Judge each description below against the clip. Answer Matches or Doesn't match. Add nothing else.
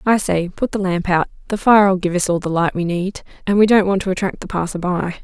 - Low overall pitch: Doesn't match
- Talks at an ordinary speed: Doesn't match